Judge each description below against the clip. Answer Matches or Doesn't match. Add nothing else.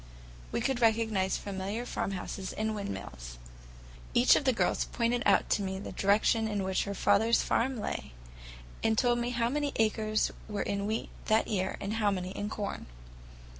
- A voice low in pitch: Doesn't match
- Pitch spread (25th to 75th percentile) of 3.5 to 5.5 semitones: Doesn't match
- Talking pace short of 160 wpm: Doesn't match